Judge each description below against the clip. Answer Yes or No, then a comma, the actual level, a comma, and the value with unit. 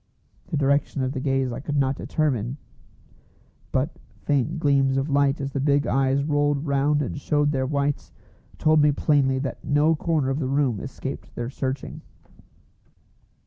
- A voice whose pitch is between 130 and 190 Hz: Yes, medium, 140 Hz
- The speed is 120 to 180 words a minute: Yes, average, 160 wpm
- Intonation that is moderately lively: No, narrow, 1.6 semitones